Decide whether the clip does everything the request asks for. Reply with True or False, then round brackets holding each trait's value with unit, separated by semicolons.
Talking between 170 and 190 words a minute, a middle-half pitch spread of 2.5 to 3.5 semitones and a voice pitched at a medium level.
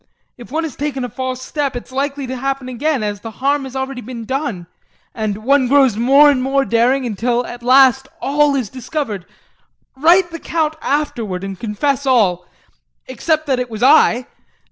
False (180 wpm; 3.1 semitones; 260 Hz)